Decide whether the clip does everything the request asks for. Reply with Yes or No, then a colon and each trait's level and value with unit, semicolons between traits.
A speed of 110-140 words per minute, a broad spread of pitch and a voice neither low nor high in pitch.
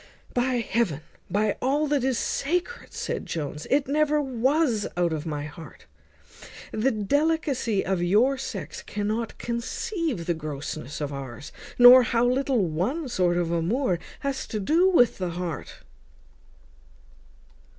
No: slow, 135 wpm; wide, 8.0 semitones; high, 230 Hz